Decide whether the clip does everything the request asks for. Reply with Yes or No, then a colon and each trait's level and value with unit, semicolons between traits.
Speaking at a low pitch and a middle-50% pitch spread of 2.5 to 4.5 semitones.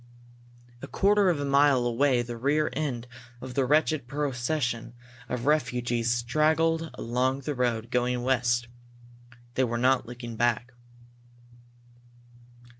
Yes: low, 125 Hz; average, 3.1 semitones